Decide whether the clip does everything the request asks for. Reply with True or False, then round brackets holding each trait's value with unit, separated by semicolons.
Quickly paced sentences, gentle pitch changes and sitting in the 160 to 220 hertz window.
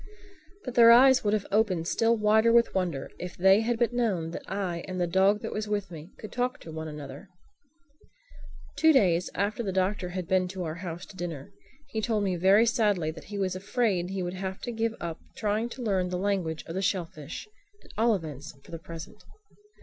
False (210 wpm; 4.0 semitones; 190 Hz)